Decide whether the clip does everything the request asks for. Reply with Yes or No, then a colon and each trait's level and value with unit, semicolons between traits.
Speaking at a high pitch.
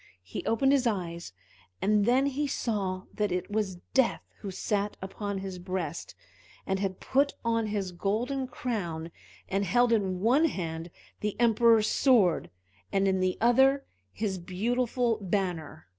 Yes: high, 205 Hz